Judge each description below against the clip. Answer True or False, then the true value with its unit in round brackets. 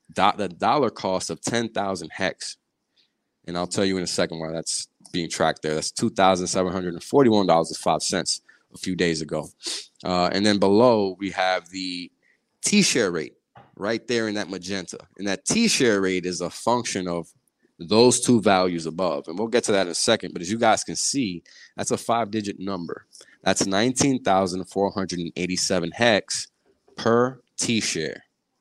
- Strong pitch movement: False (3.4 semitones)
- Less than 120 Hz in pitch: True (95 Hz)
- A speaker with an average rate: True (165 wpm)